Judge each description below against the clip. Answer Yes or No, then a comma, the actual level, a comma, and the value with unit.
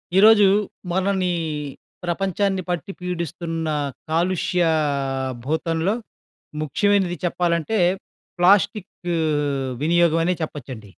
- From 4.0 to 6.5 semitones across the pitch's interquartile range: No, average, 2.8 semitones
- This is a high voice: No, medium, 175 Hz